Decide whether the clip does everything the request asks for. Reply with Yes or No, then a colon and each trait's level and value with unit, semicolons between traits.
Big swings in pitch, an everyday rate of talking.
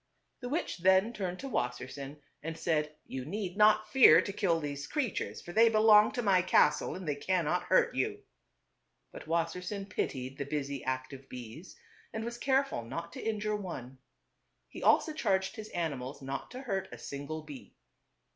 Yes: wide, 7.0 semitones; average, 170 wpm